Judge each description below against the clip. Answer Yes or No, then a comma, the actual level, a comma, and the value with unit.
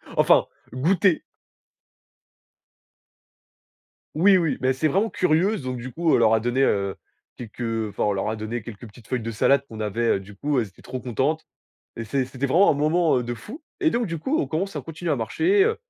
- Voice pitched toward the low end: Yes, low, 130 Hz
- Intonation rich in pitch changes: Yes, wide, 6.9 semitones